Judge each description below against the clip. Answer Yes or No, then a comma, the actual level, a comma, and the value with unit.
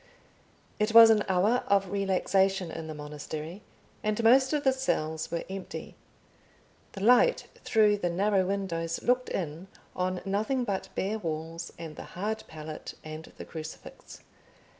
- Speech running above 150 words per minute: No, average, 145 wpm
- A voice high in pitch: Yes, high, 195 Hz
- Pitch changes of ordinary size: Yes, average, 4.5 semitones